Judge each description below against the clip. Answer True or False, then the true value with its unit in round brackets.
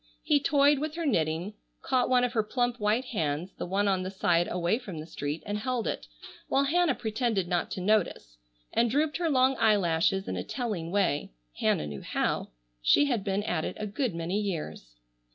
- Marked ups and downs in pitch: True (6.6 semitones)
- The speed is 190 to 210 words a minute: True (200 wpm)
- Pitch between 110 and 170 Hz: False (210 Hz)